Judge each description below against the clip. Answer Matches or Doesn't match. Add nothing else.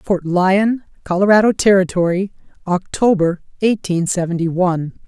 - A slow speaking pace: Matches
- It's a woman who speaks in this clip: Matches